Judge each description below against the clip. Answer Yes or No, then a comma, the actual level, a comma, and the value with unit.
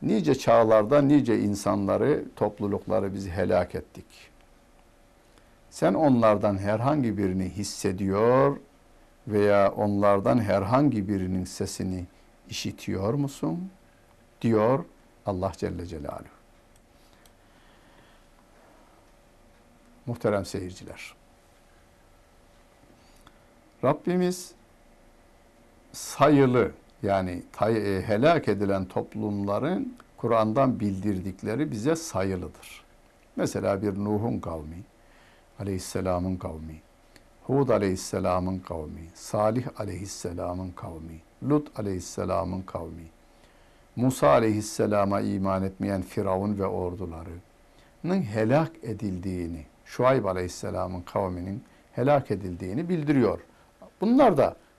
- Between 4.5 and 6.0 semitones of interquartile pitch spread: No, average, 3.9 semitones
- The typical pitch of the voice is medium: No, low, 100 Hz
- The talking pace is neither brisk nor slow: No, slow, 75 wpm